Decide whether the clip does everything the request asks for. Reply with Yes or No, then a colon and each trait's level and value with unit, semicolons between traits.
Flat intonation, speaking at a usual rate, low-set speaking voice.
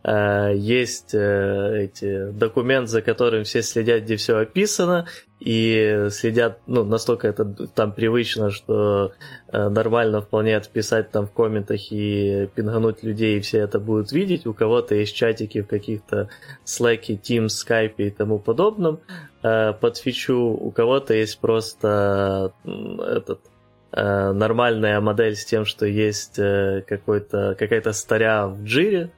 Yes: narrow, 2.0 semitones; average, 125 wpm; low, 110 Hz